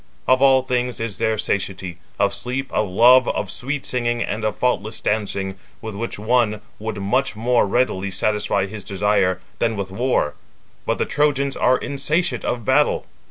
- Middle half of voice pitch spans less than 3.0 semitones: No, average, 3.9 semitones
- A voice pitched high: No, low, 110 Hz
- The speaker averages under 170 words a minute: Yes, average, 160 wpm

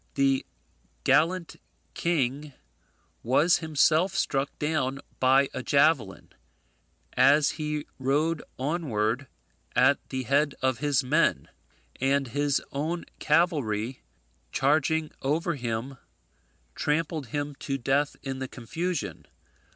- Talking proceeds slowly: Yes, slow, 105 wpm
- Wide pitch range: No, average, 2.9 semitones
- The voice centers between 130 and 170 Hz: Yes, medium, 140 Hz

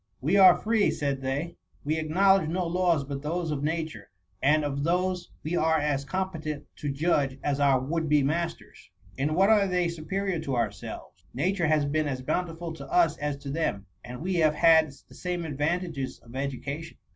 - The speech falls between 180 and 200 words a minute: Yes, average, 190 wpm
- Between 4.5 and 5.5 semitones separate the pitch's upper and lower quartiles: No, average, 3.8 semitones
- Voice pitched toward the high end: No, medium, 155 Hz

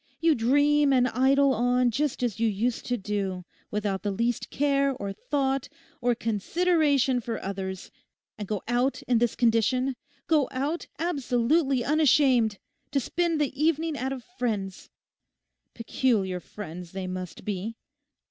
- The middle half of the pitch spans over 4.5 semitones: Yes, average, 4.9 semitones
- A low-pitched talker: No, high, 245 Hz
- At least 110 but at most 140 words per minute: Yes, slow, 135 wpm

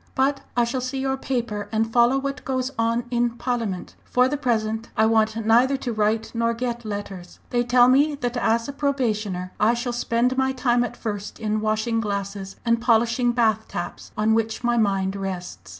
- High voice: Yes, high, 230 Hz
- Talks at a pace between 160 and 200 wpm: Yes, average, 190 wpm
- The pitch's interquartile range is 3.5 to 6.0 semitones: No, narrow, 2.5 semitones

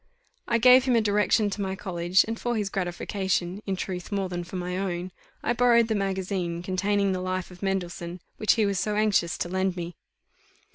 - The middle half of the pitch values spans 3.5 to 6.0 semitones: No, narrow, 2.6 semitones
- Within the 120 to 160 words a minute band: No, average, 200 wpm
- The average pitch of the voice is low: No, high, 190 Hz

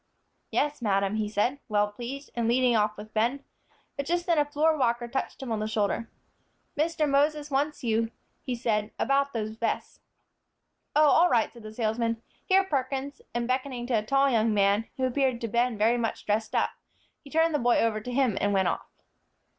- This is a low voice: No, high, 240 Hz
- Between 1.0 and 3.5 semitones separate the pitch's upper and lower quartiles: No, average, 4.3 semitones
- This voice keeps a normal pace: Yes, average, 195 wpm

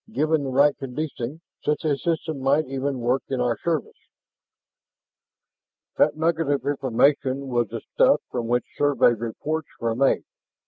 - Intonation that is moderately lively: Yes, average, 3.5 semitones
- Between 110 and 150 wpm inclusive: Yes, average, 145 wpm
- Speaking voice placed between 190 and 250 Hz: No, medium, 140 Hz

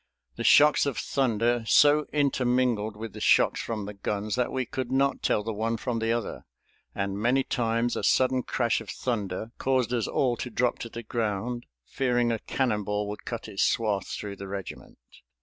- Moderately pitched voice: No, low, 115 Hz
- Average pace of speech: Yes, average, 185 wpm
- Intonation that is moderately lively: Yes, average, 3.2 semitones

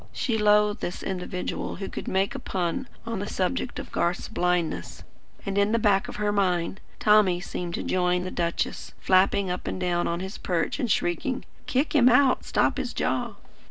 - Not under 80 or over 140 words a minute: No, average, 190 wpm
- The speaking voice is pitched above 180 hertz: Yes, high, 190 Hz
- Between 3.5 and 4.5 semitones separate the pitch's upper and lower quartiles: No, average, 2.9 semitones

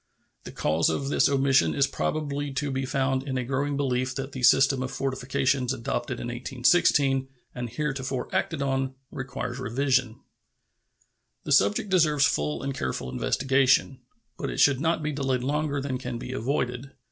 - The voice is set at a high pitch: No, low, 135 Hz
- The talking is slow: No, average, 165 wpm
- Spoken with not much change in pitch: Yes, narrow, 1.9 semitones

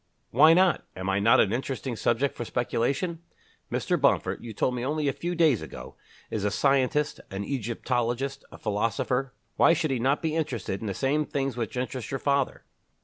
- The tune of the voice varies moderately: Yes, average, 3.6 semitones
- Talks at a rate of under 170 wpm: No, average, 190 wpm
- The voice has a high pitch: No, low, 130 Hz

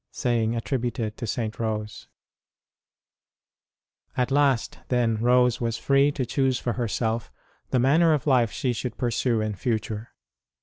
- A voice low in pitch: Yes, low, 120 Hz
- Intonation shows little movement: Yes, narrow, 2.3 semitones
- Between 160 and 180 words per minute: No, slow, 135 wpm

